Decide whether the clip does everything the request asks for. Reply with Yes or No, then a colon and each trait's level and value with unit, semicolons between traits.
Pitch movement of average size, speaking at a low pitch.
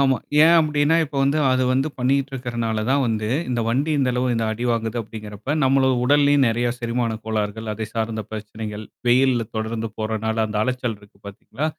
Yes: average, 3.3 semitones; low, 120 Hz